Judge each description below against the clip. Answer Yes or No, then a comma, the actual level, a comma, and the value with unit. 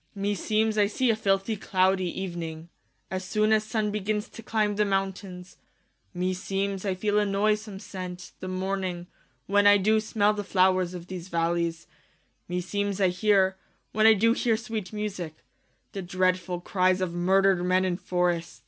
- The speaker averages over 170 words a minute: Yes, average, 185 wpm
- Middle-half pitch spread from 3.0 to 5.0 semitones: No, narrow, 2.4 semitones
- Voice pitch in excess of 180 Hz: Yes, high, 190 Hz